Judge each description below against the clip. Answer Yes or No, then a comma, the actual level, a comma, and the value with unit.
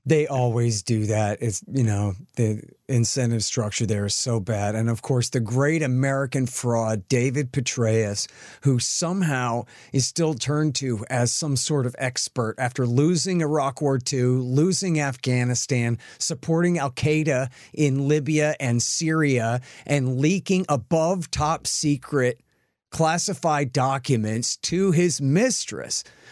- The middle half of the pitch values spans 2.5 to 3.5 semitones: No, average, 4.1 semitones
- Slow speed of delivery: Yes, slow, 130 wpm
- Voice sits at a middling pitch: No, low, 130 Hz